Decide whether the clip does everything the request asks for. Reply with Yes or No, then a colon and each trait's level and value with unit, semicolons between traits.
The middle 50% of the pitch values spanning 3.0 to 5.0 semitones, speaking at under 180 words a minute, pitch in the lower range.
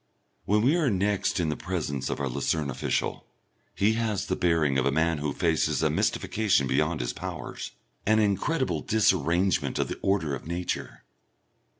No: wide, 5.6 semitones; average, 170 wpm; very low, 85 Hz